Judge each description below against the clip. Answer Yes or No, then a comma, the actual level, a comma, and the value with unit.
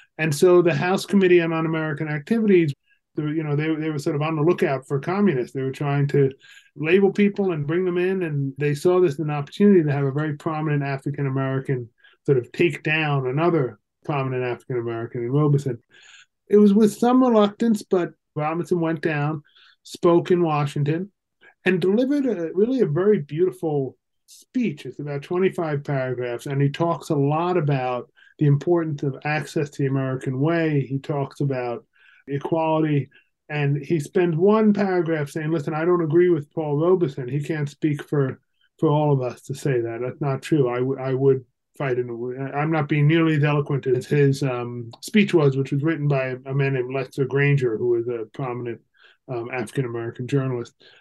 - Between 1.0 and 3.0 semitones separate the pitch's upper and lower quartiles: No, average, 4.2 semitones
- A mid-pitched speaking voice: Yes, medium, 150 Hz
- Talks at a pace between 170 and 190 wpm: Yes, average, 185 wpm